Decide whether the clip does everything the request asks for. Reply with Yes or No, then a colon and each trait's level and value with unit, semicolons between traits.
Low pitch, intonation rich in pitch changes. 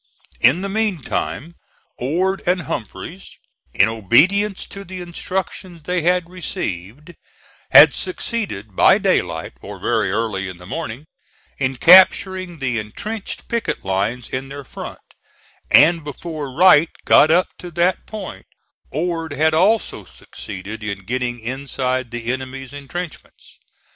No: medium, 150 Hz; wide, 7.0 semitones